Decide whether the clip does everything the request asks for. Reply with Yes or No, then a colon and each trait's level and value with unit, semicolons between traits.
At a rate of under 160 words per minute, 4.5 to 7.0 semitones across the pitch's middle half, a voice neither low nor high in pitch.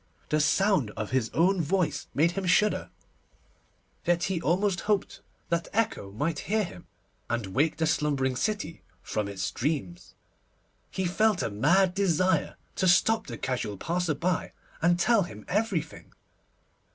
Yes: average, 145 wpm; average, 5.1 semitones; medium, 170 Hz